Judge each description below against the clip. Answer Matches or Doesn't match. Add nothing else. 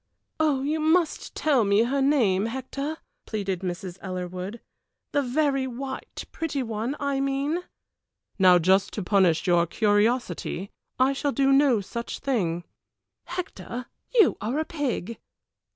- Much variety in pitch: Matches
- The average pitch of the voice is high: Matches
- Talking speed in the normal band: Doesn't match